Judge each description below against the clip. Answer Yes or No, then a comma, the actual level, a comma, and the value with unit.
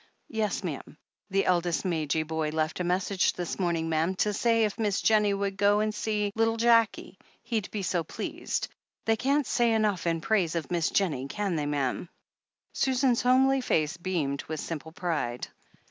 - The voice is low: No, high, 190 Hz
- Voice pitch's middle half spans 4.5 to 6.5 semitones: Yes, average, 5.2 semitones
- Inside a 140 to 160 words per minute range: No, average, 175 wpm